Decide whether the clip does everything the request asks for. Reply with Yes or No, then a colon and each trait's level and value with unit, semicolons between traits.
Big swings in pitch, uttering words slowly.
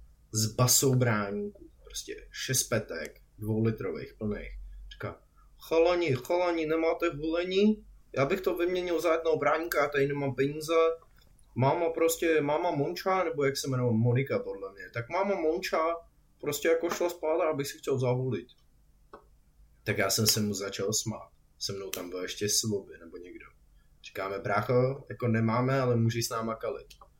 No: wide, 6.9 semitones; average, 155 wpm